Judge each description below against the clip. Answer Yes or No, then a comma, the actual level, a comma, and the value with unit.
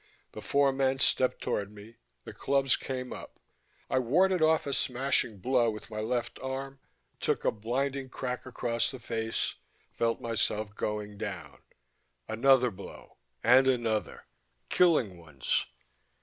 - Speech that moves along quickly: No, slow, 135 wpm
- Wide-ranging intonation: No, average, 3.5 semitones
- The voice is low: Yes, low, 125 Hz